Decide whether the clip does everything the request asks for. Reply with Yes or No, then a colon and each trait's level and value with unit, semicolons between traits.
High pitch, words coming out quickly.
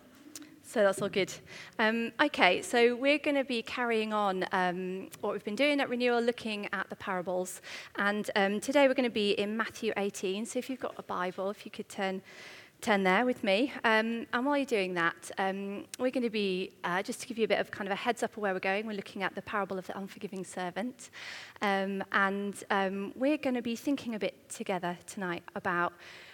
Yes: high, 205 Hz; fast, 225 wpm